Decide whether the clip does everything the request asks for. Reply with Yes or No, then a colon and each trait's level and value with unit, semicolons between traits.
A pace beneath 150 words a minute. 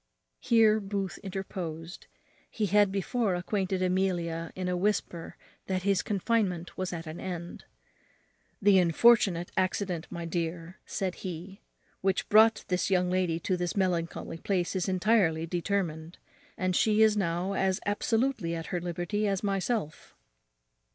Yes: average, 140 wpm